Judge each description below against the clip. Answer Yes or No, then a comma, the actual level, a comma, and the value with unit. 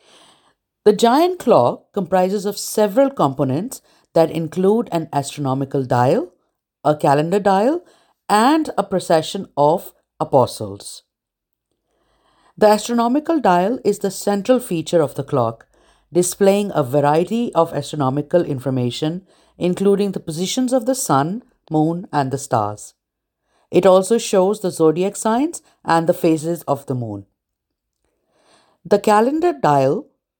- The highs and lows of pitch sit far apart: Yes, wide, 6.0 semitones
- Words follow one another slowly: Yes, slow, 120 wpm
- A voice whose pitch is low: No, medium, 180 Hz